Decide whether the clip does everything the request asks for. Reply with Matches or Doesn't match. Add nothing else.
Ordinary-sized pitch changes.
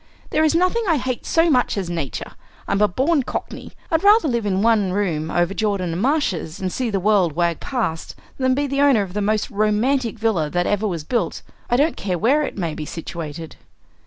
Doesn't match